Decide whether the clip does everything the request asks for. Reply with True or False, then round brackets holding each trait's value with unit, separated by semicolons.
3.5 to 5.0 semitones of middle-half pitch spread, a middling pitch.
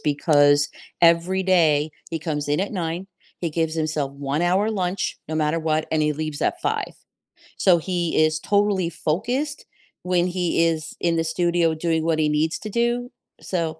False (2.7 semitones; 165 Hz)